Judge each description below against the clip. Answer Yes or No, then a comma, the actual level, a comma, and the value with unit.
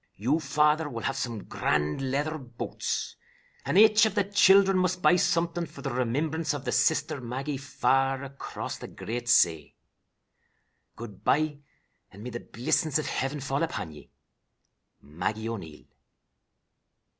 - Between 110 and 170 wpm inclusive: Yes, average, 145 wpm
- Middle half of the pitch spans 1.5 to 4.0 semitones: No, average, 5.3 semitones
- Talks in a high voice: No, low, 135 Hz